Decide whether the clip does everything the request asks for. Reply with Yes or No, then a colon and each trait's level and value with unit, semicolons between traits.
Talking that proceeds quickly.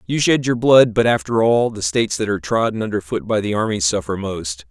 Yes: fast, 240 wpm